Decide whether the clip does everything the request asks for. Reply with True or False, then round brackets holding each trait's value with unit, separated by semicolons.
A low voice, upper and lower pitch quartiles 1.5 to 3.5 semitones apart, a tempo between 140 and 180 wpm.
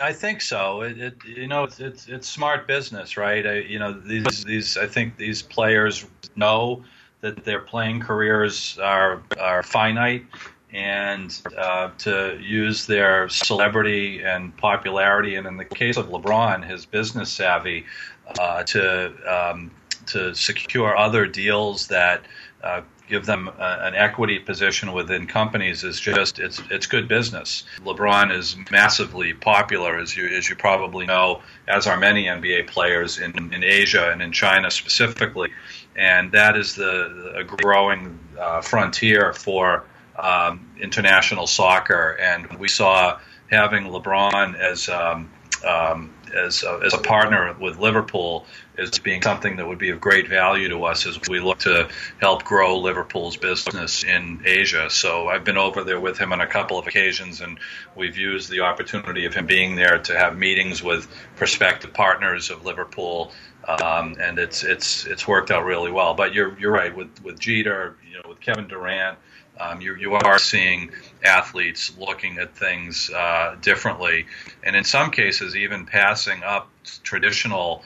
True (100 Hz; 2.9 semitones; 160 wpm)